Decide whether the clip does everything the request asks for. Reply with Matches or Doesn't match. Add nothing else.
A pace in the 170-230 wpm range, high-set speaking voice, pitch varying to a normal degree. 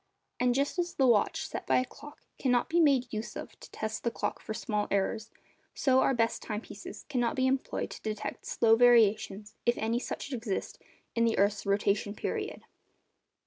Matches